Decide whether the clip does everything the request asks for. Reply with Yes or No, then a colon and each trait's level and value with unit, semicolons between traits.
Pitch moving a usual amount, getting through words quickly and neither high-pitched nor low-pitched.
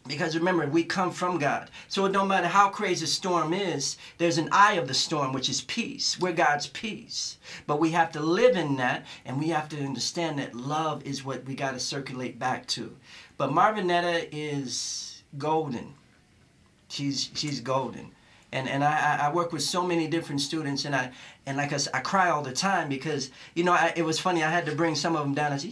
Yes: average, 4.0 semitones; fast, 210 wpm; medium, 150 Hz